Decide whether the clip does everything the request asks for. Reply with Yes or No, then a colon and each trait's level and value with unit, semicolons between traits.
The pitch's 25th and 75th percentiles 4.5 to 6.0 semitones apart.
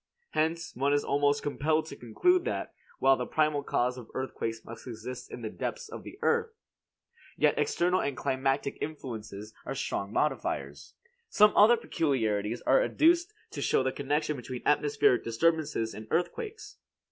Yes: average, 5.2 semitones